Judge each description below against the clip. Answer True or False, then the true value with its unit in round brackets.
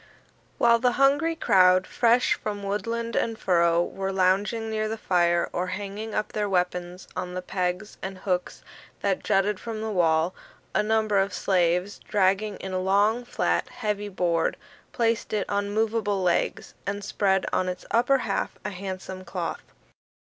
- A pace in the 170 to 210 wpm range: False (160 wpm)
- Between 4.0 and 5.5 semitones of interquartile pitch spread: False (2.9 semitones)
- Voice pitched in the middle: False (200 Hz)